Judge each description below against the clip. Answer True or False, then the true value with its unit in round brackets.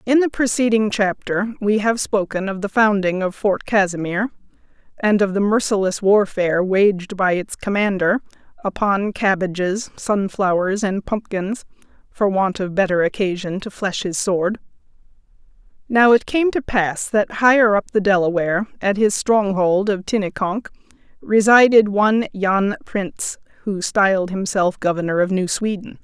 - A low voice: False (200 Hz)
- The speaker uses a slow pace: False (145 wpm)